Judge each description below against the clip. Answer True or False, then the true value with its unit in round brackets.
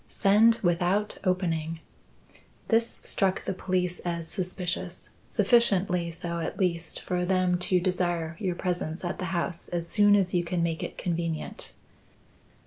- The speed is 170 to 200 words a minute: False (140 wpm)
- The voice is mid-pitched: True (180 Hz)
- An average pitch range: False (1.9 semitones)